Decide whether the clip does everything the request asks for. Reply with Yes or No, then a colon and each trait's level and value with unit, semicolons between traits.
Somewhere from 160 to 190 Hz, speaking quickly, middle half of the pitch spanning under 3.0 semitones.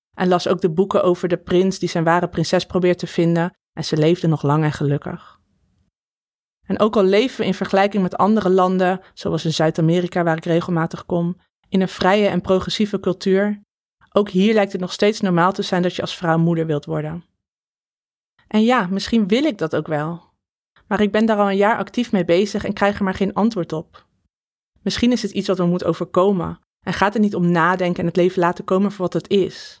Yes: medium, 185 Hz; fast, 220 wpm; narrow, 2.5 semitones